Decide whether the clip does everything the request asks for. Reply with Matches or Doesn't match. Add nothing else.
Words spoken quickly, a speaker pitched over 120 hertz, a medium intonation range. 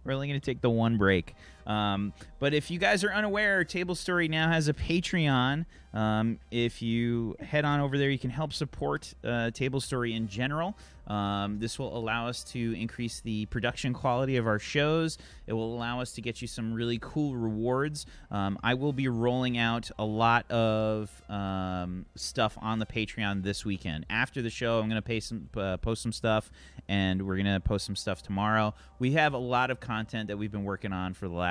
Doesn't match